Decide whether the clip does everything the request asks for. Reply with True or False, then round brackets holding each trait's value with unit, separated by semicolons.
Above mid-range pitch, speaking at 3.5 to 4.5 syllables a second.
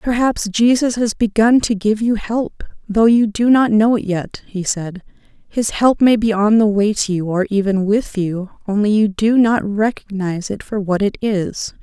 True (210 Hz; 4.4 syllables/s)